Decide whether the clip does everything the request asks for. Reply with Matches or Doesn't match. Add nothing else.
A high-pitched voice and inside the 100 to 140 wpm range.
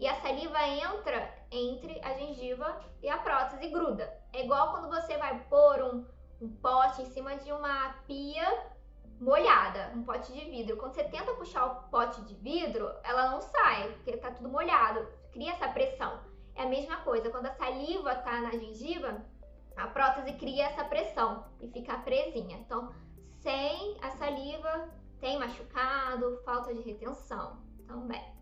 Doesn't match